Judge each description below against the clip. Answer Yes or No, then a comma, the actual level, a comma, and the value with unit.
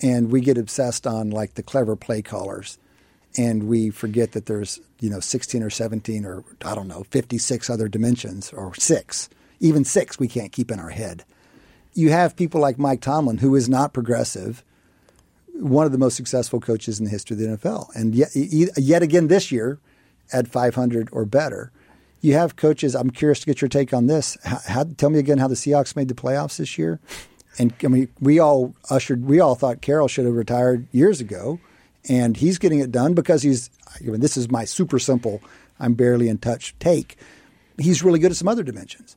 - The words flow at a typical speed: No, fast, 210 wpm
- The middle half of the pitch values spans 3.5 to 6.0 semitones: Yes, average, 3.9 semitones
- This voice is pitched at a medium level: No, low, 125 Hz